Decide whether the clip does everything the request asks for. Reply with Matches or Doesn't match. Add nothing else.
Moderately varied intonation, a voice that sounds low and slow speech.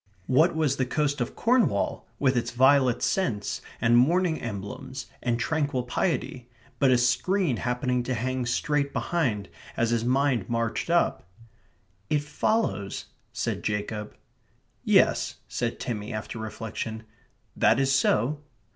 Matches